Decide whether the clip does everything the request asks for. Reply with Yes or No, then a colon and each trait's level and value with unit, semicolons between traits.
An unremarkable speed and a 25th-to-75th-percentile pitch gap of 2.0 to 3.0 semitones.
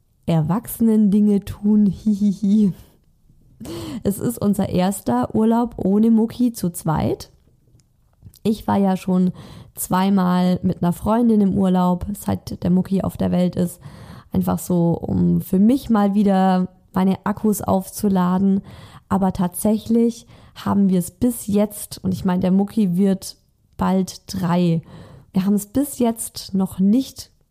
Yes: average, 140 wpm; average, 2.7 semitones